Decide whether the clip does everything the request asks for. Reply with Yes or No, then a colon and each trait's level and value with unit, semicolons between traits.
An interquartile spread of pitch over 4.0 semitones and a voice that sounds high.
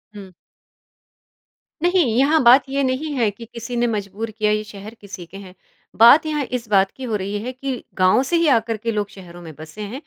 Yes: average, 4.4 semitones; high, 225 Hz